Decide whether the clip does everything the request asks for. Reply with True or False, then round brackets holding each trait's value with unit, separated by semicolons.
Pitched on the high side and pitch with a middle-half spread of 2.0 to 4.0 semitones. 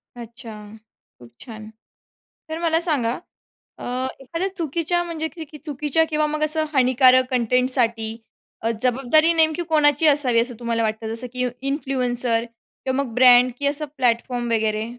False (255 Hz; 4.6 semitones)